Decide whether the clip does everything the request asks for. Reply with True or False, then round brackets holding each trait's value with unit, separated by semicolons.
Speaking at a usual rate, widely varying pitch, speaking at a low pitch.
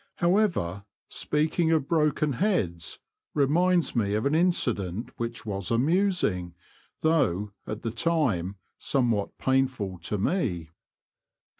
False (115 wpm; 8.3 semitones; 125 Hz)